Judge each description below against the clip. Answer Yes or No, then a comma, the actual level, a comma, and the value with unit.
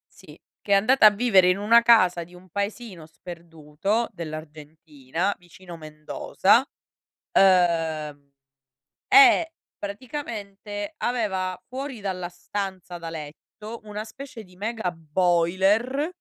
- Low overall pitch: No, high, 190 Hz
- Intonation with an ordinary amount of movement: Yes, average, 4.7 semitones